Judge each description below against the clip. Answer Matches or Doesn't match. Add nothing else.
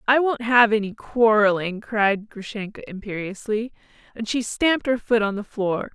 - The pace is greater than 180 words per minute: Doesn't match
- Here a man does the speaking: Doesn't match